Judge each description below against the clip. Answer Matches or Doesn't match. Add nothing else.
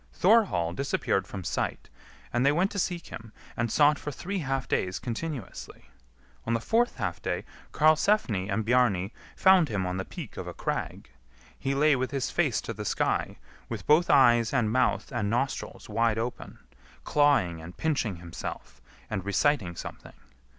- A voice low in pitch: Matches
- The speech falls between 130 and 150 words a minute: Doesn't match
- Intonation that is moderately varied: Doesn't match